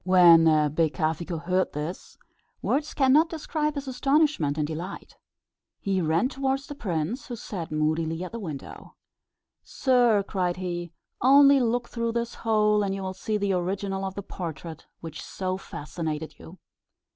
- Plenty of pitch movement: Yes, wide, 6.8 semitones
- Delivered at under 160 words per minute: Yes, average, 150 wpm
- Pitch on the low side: No, high, 190 Hz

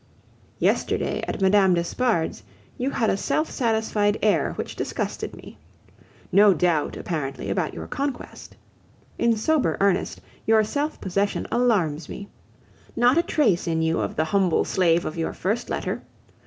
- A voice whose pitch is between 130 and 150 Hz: No, high, 200 Hz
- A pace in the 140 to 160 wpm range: Yes, average, 145 wpm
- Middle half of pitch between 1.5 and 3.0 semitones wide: No, wide, 5.6 semitones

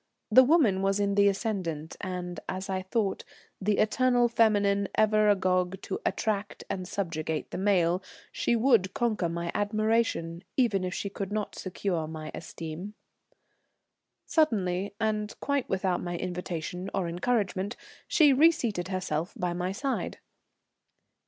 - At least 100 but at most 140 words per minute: Yes, slow, 135 wpm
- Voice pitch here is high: Yes, high, 195 Hz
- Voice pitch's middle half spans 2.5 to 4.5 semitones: Yes, average, 3.3 semitones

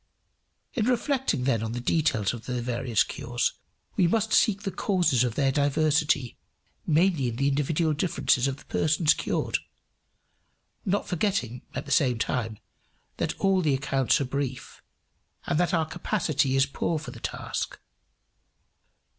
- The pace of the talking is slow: No, average, 150 wpm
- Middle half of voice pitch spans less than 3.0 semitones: No, wide, 5.5 semitones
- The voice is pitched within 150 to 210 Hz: No, medium, 140 Hz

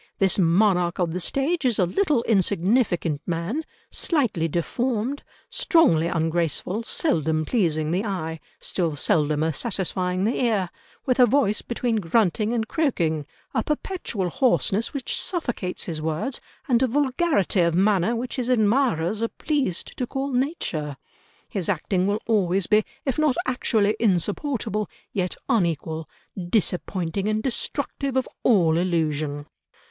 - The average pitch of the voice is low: No, high, 200 Hz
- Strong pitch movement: Yes, wide, 6.6 semitones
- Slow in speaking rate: Yes, slow, 130 wpm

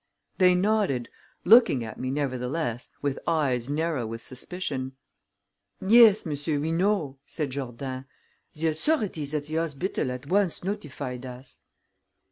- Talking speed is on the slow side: Yes, slow, 125 wpm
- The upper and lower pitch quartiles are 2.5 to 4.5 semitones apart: No, wide, 5.6 semitones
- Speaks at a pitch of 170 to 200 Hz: No, medium, 145 Hz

